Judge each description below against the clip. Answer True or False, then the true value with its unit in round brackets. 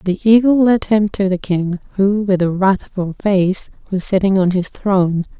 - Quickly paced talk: False (190 wpm)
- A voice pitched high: True (195 Hz)